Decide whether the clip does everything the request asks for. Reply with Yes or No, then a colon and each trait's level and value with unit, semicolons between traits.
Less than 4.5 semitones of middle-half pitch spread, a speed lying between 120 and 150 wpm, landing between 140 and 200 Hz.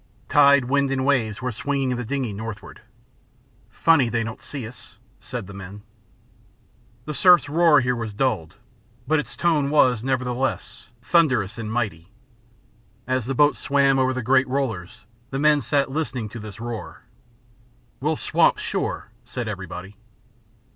No: average, 4.0 semitones; average, 145 wpm; low, 125 Hz